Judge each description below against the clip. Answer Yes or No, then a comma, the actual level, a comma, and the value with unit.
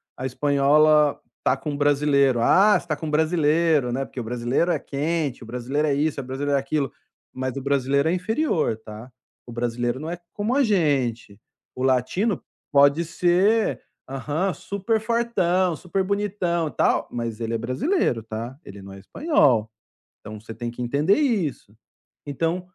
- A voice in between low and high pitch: Yes, medium, 145 Hz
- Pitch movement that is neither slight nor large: No, wide, 5.9 semitones